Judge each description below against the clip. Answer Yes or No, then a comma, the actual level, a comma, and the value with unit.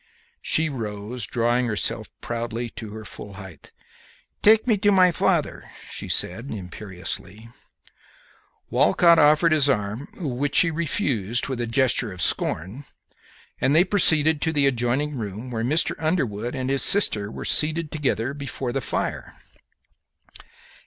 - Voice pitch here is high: No, low, 125 Hz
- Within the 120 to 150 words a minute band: Yes, average, 140 wpm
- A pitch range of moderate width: No, wide, 5.7 semitones